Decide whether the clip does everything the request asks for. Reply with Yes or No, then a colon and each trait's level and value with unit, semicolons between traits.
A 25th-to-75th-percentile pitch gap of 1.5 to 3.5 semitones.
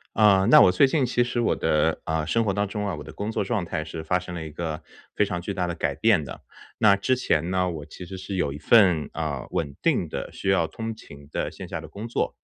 No: average, 4.7 semitones